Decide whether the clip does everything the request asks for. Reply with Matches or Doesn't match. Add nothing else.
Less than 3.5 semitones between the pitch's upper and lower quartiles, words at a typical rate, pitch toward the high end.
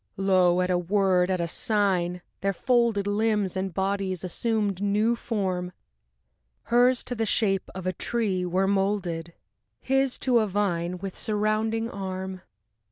Matches